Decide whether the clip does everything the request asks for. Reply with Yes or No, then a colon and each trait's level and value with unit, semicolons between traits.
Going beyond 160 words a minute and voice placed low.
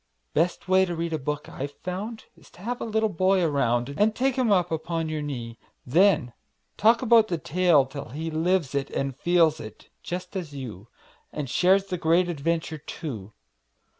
No: average, 180 wpm; medium, 165 Hz